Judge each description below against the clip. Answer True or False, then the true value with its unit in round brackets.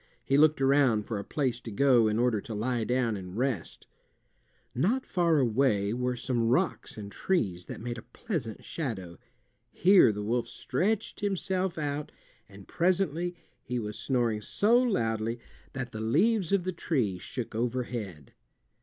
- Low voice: True (125 Hz)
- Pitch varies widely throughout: True (6.8 semitones)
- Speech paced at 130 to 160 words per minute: True (155 wpm)